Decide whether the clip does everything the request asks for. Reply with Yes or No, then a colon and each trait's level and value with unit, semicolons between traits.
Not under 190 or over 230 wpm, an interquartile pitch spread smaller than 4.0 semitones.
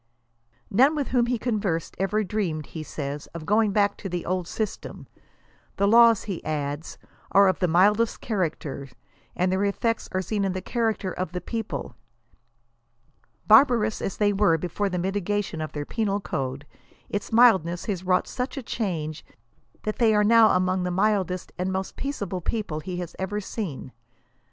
No: average, 170 wpm; average, 3.5 semitones